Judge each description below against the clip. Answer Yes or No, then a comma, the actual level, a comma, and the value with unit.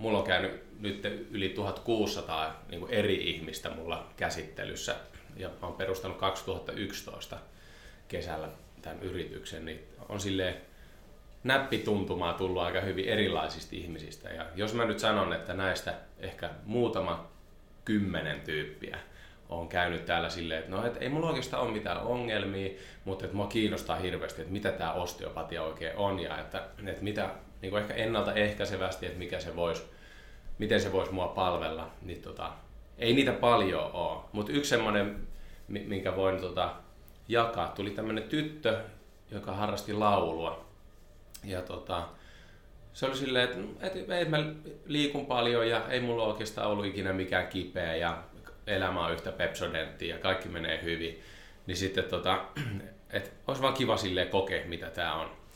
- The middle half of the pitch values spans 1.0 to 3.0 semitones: No, average, 3.6 semitones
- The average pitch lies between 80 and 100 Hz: Yes, very low, 95 Hz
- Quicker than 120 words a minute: Yes, average, 145 wpm